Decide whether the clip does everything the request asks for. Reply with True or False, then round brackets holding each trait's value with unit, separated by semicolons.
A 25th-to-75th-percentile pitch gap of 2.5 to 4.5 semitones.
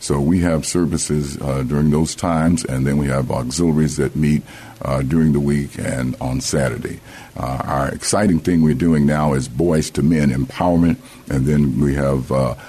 True (3.0 semitones)